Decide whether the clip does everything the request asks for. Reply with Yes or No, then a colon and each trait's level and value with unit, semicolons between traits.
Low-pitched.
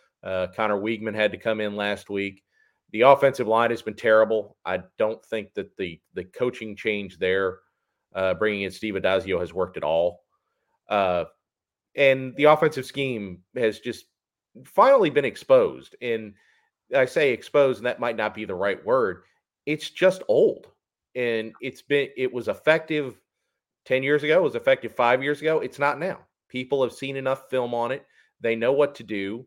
Yes: low, 120 Hz